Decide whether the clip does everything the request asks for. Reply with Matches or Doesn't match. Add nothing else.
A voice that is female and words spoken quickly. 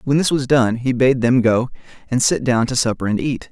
Doesn't match